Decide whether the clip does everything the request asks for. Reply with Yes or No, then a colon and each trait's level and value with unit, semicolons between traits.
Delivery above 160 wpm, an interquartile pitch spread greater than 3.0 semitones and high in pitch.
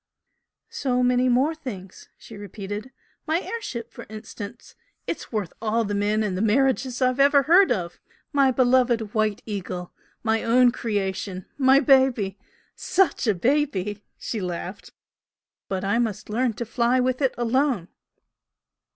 No: average, 150 wpm; average, 4.1 semitones; high, 235 Hz